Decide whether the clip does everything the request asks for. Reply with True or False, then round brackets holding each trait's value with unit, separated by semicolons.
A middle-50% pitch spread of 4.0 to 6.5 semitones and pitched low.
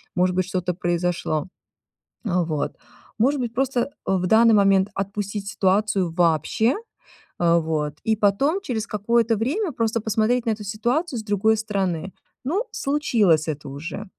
False (4.4 semitones; 205 Hz)